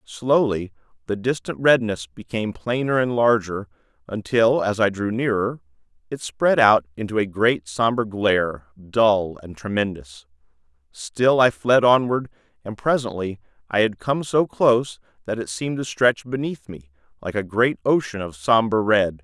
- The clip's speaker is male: Yes, male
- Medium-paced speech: Yes, average, 150 wpm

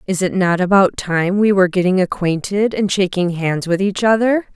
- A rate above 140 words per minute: Yes, average, 200 wpm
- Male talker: No, female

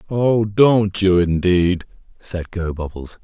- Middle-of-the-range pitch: No, very low, 95 Hz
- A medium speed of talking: No, slow, 110 wpm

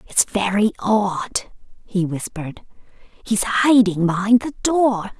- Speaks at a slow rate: Yes, slow, 115 wpm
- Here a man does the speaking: No, female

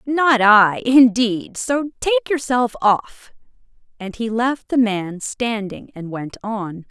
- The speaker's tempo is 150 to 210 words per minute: No, average, 140 wpm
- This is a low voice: No, high, 230 Hz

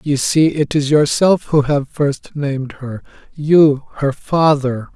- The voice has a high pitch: No, medium, 145 Hz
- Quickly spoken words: No, average, 145 wpm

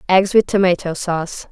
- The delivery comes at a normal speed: Yes, average, 160 wpm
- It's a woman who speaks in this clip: Yes, female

